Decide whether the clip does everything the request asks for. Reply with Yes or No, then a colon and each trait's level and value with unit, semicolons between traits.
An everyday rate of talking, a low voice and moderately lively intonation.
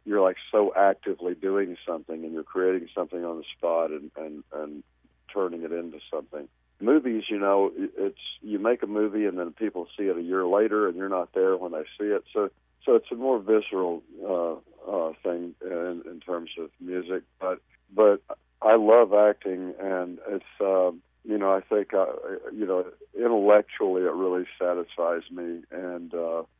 Yes: average, 185 wpm; very low, 90 Hz; average, 4.0 semitones